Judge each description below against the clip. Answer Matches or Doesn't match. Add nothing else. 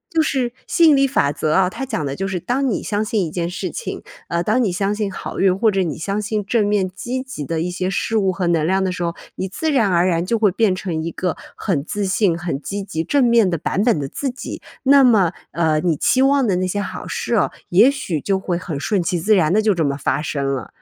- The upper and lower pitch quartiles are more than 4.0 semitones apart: Matches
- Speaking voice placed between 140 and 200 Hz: Matches